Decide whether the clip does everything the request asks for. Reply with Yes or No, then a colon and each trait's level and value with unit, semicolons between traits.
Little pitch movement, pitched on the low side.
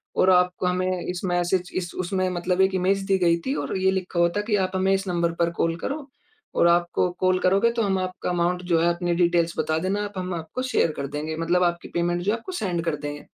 No: narrow, 1.7 semitones; medium, 180 Hz